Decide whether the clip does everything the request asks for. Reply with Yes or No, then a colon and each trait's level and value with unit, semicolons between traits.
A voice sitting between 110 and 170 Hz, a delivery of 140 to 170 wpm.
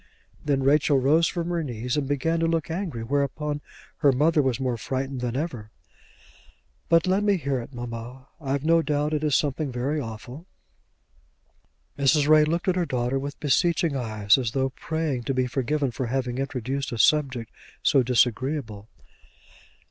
Yes: medium, 140 Hz; average, 165 wpm